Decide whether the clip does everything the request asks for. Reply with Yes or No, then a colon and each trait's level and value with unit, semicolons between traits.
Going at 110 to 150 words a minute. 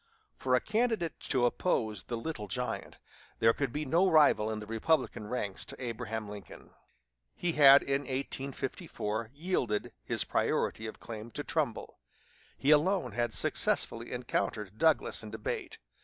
Yes: average, 145 wpm